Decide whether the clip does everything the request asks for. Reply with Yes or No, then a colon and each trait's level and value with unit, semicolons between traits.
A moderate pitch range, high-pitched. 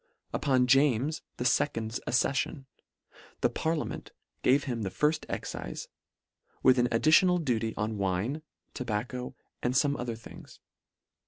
No: average, 4.1 semitones; low, 125 Hz